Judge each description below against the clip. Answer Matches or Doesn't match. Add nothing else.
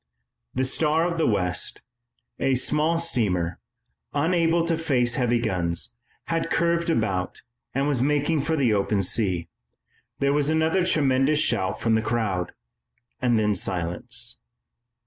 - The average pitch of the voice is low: Matches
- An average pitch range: Doesn't match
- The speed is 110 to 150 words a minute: Matches